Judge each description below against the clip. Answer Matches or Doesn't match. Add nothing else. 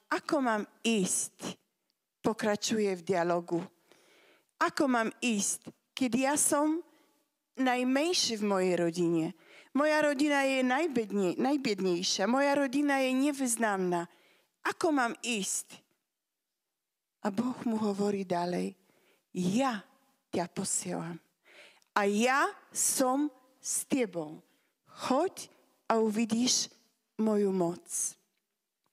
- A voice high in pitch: Matches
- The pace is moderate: Doesn't match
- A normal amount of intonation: Doesn't match